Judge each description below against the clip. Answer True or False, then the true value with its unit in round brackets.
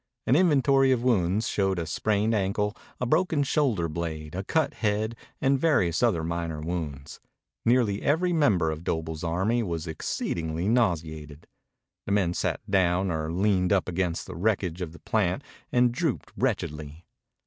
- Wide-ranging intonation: True (6.2 semitones)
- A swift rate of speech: False (155 wpm)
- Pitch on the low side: True (95 Hz)